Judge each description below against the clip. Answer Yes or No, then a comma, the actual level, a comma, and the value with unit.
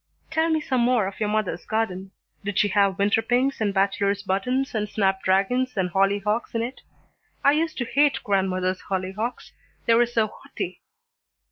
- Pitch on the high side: Yes, high, 210 Hz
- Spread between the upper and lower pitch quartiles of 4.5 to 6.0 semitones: No, average, 3.9 semitones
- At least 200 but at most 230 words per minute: No, average, 170 wpm